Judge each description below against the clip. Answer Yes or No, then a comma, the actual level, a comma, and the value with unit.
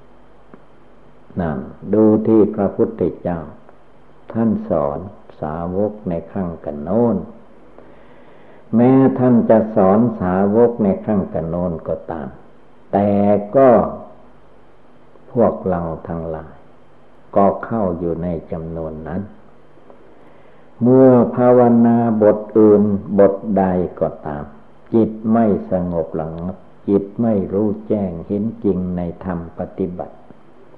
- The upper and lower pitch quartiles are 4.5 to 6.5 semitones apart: Yes, average, 4.9 semitones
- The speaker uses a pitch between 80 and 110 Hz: Yes, low, 100 Hz